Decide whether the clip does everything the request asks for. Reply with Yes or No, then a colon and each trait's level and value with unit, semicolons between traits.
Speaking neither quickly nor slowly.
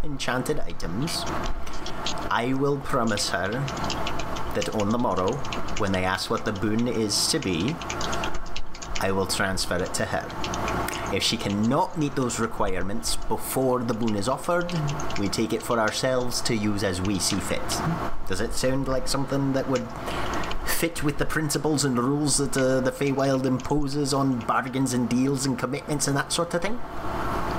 Yes: average, 165 wpm